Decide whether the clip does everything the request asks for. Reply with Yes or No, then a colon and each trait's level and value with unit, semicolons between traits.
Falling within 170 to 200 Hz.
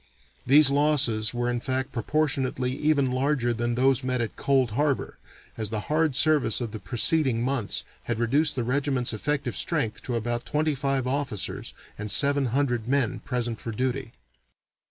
No: low, 130 Hz